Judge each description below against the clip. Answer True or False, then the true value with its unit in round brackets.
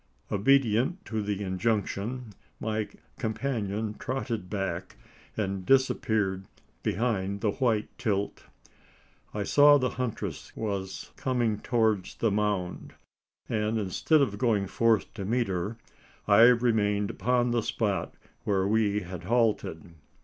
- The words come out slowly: True (120 wpm)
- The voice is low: True (110 Hz)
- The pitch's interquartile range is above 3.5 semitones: False (3.0 semitones)